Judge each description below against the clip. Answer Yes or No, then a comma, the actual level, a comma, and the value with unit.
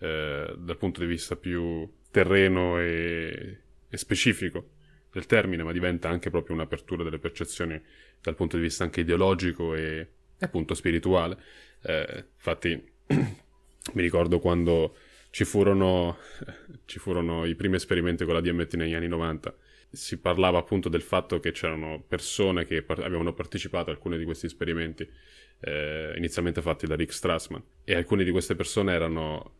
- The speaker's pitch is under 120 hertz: Yes, very low, 85 Hz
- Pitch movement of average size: No, narrow, 1.3 semitones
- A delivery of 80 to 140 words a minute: No, average, 150 wpm